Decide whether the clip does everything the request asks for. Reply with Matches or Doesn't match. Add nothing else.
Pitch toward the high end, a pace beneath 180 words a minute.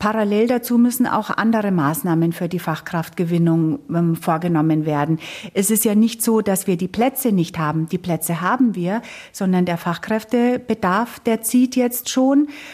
Matches